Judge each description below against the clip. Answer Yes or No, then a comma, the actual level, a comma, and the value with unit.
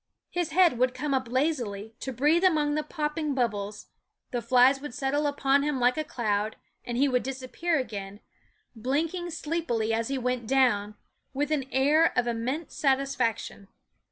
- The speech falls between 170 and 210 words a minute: No, average, 160 wpm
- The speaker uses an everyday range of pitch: Yes, average, 4.0 semitones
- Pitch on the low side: No, very high, 265 Hz